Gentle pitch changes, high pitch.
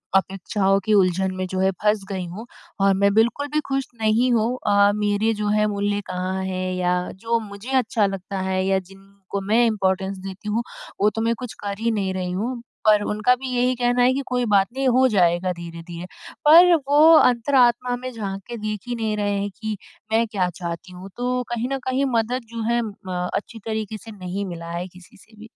No: average, 3.7 semitones; high, 210 Hz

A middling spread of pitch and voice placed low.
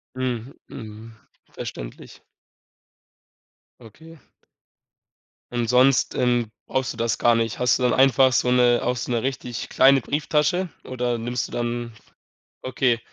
No: narrow, 1.9 semitones; low, 125 Hz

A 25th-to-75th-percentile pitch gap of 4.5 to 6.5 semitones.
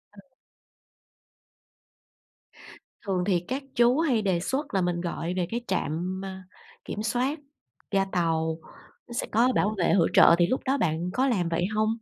Yes: wide, 5.6 semitones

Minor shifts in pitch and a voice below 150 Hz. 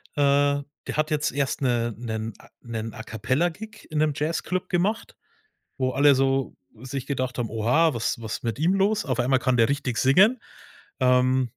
No: average, 4.1 semitones; low, 135 Hz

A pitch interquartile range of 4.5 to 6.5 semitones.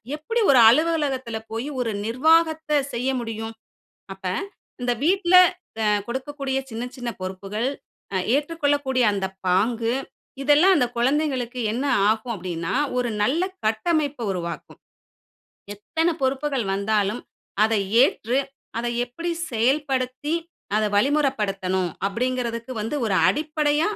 Yes: average, 4.9 semitones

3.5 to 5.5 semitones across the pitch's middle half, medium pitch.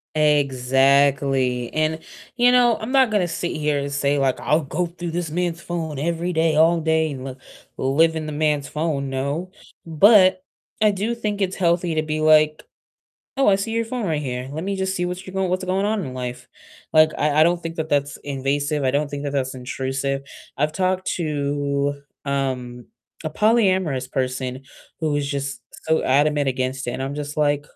Yes: average, 4.1 semitones; medium, 150 Hz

